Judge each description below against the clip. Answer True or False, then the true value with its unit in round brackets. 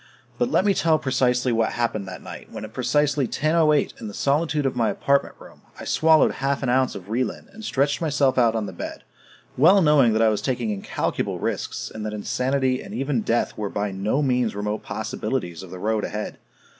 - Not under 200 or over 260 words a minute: True (205 wpm)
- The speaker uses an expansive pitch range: False (4.7 semitones)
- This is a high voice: False (125 Hz)